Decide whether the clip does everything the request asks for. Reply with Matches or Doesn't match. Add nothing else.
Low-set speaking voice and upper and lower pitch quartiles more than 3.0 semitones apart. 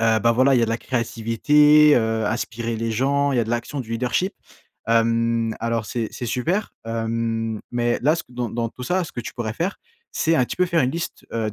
Matches